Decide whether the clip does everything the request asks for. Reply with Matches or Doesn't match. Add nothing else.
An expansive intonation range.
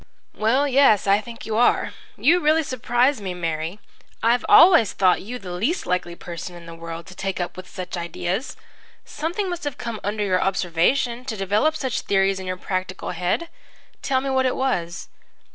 Matches